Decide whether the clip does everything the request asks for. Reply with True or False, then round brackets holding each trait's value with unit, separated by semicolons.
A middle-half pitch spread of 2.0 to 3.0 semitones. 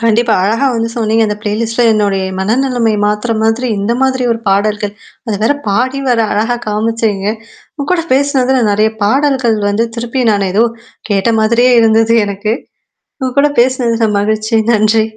True (2.6 semitones)